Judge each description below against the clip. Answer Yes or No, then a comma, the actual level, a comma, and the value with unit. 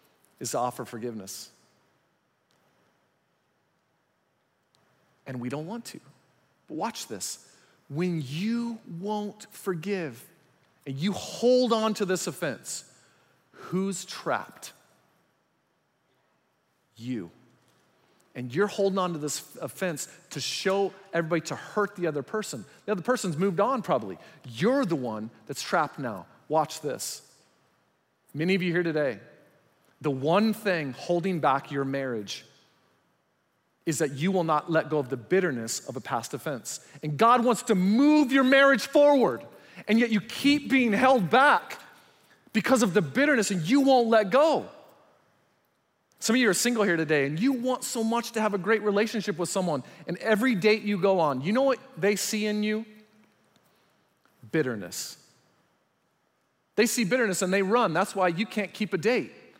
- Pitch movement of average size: No, wide, 6.2 semitones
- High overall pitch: Yes, high, 195 Hz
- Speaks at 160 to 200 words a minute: No, average, 150 wpm